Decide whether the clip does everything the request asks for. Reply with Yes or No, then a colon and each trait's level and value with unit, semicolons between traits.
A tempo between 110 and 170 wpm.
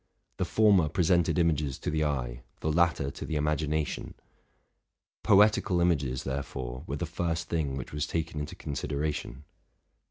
Yes: average, 145 wpm